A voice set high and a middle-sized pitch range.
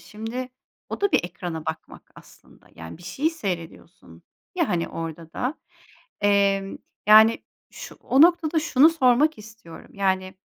No: high, 210 Hz; wide, 7.8 semitones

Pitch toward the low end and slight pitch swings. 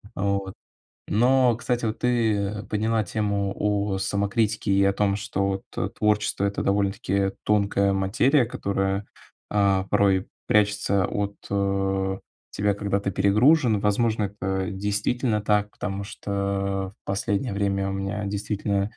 Yes: low, 100 Hz; narrow, 1.3 semitones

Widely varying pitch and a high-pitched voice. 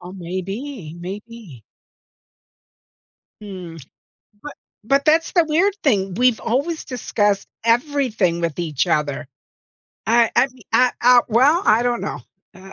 Yes: wide, 6.3 semitones; high, 225 Hz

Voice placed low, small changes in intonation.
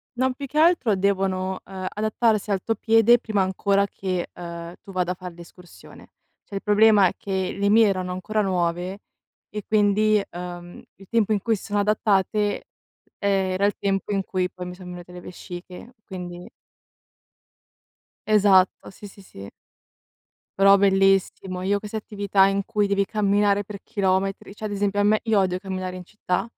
No: high, 195 Hz; narrow, 2.2 semitones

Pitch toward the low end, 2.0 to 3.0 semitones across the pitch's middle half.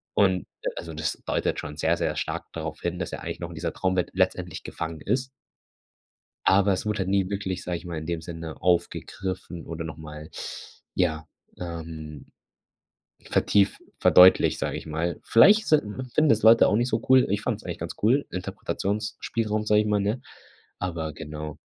No: very low, 90 Hz; average, 4.4 semitones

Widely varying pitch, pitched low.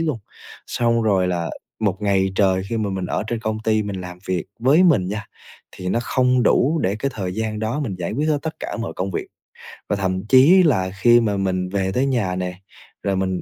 No: average, 4.3 semitones; low, 105 Hz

